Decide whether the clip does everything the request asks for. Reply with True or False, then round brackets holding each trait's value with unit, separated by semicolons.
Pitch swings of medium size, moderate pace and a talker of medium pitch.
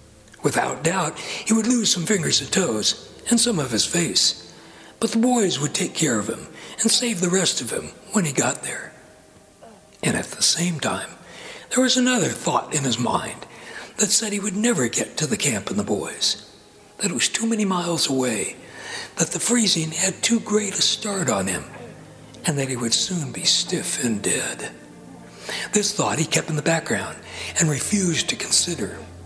False (7.0 semitones; 190 wpm; 180 Hz)